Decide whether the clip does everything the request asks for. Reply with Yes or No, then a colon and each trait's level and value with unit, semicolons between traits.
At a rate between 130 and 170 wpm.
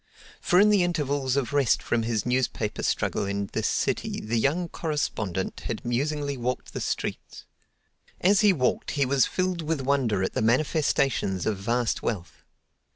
Yes: average, 160 wpm